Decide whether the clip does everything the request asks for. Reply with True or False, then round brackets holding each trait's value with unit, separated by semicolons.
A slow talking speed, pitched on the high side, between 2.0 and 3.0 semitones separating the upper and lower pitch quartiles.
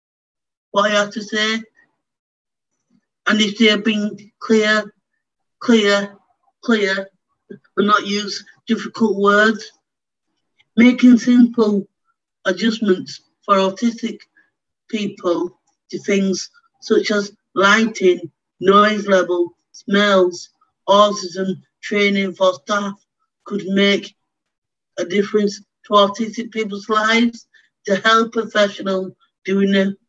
True (100 wpm; 205 Hz; 2.4 semitones)